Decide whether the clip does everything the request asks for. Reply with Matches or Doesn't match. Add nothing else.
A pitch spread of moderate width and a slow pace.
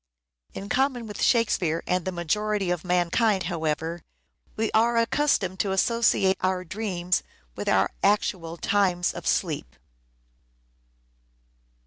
Matches